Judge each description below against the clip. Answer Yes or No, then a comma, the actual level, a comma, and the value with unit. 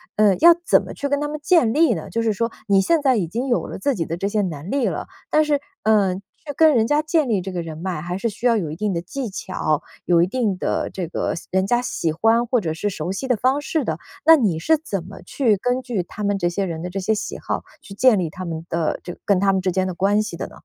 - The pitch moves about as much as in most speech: No, wide, 5.7 semitones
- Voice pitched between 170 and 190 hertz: No, high, 205 Hz